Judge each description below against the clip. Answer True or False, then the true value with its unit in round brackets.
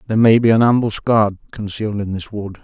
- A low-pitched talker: True (105 Hz)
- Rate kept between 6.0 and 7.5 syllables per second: True (6.2 syllables/s)